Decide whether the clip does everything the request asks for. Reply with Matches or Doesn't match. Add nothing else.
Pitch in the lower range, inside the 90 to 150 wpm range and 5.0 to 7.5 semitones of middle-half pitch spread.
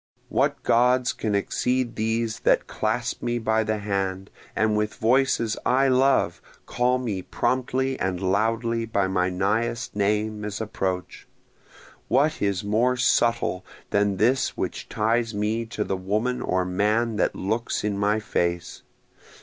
Doesn't match